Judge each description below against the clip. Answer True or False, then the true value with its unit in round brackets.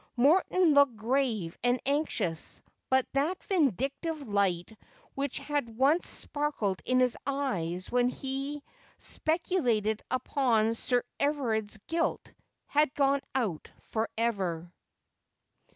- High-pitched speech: True (255 Hz)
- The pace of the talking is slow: True (105 wpm)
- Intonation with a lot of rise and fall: False (4.6 semitones)